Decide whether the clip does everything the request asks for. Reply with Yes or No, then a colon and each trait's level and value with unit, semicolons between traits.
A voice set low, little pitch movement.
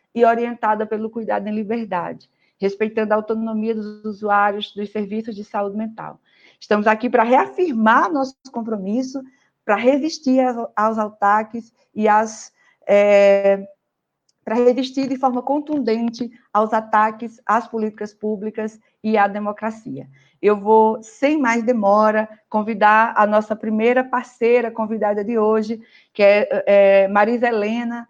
No: high, 220 Hz; narrow, 2.1 semitones